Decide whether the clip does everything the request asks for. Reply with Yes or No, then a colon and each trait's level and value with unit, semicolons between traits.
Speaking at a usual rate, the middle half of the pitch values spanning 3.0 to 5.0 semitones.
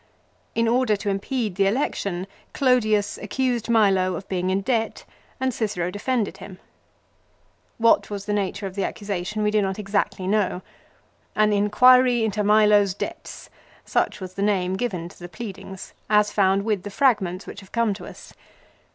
No: average, 170 wpm; narrow, 2.5 semitones